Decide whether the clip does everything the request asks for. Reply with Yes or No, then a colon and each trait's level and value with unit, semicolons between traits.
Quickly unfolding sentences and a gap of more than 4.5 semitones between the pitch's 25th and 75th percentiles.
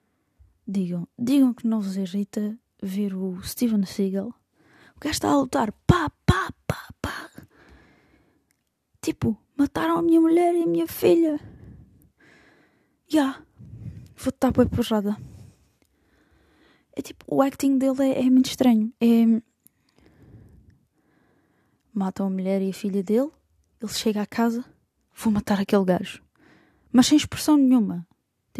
No: average, 125 wpm; average, 5.1 semitones